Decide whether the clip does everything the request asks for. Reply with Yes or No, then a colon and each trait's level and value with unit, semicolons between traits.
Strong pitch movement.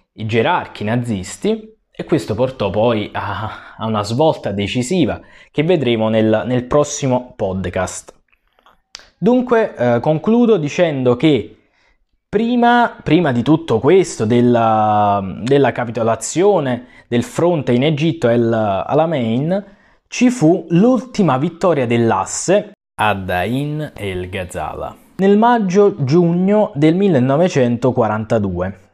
Yes: wide, 7.8 semitones